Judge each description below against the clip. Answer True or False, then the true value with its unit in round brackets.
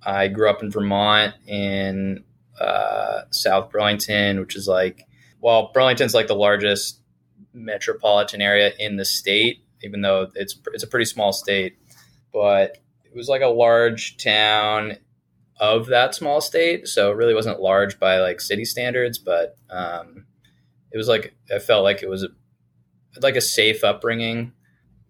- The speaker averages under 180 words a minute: True (155 wpm)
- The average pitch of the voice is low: True (105 Hz)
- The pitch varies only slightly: False (3.2 semitones)